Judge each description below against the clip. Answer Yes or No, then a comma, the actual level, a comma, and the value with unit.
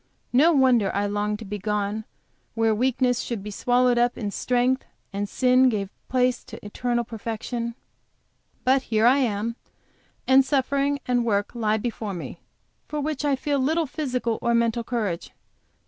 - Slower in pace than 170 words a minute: Yes, average, 160 wpm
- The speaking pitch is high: Yes, high, 240 Hz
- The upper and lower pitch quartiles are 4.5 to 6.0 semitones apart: No, average, 3.3 semitones